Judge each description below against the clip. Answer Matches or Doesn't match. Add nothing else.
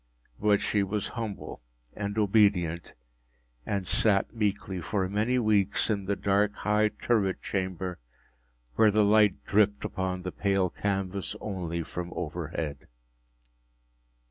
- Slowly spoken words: Matches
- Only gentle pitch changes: Matches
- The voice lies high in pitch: Doesn't match